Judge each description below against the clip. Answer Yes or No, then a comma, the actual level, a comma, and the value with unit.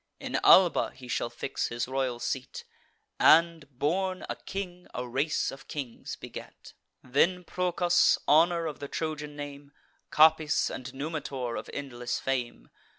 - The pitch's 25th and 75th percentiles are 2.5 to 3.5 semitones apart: No, average, 4.2 semitones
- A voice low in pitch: No, medium, 145 Hz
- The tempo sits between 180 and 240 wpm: No, average, 140 wpm